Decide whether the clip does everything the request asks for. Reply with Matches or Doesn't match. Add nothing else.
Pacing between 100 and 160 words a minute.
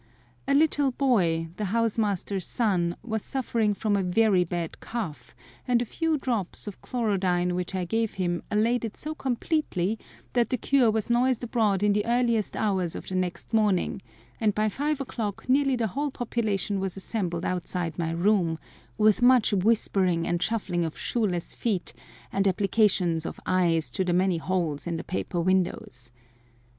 Doesn't match